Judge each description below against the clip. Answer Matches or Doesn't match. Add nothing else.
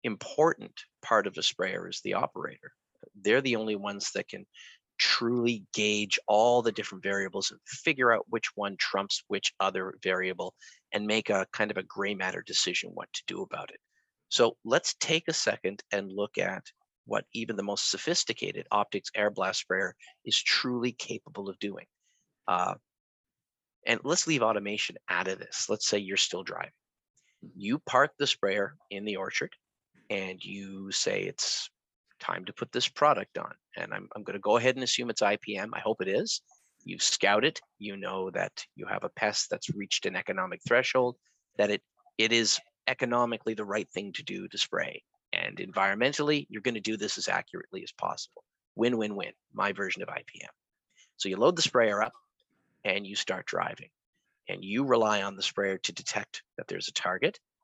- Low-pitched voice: Matches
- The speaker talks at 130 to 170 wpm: Doesn't match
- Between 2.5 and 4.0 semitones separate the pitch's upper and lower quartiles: Matches